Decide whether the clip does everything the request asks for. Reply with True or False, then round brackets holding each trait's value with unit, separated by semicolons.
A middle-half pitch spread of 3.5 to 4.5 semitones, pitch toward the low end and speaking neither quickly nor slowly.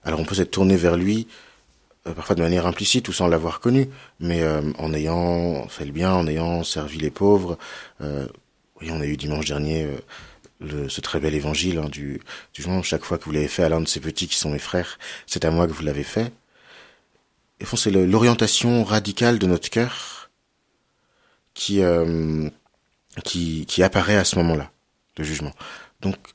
True (3.8 semitones; 85 Hz; 200 wpm)